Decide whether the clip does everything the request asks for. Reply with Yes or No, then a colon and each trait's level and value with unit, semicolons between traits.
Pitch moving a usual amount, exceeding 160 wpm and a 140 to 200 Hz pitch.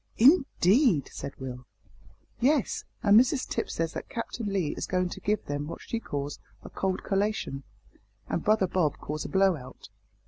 No: wide, 6.9 semitones; average, 170 wpm; high, 190 Hz